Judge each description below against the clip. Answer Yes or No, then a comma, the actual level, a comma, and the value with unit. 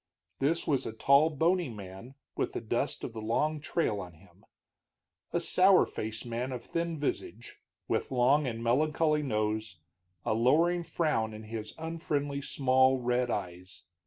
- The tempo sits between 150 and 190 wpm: Yes, average, 155 wpm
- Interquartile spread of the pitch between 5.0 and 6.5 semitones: Yes, wide, 5.6 semitones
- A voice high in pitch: No, low, 125 Hz